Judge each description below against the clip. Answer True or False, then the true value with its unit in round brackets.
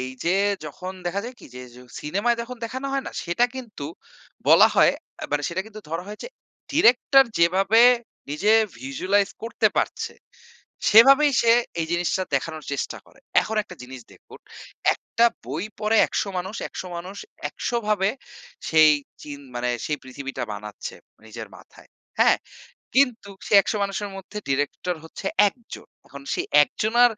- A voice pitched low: False (190 Hz)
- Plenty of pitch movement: True (7.0 semitones)